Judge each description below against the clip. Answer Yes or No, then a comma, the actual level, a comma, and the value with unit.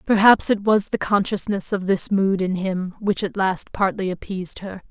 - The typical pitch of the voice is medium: No, high, 195 Hz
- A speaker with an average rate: Yes, average, 195 wpm